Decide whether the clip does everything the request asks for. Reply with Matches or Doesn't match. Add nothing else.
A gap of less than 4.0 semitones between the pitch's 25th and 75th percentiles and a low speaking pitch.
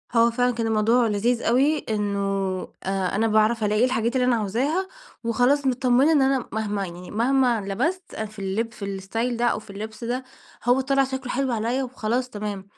Doesn't match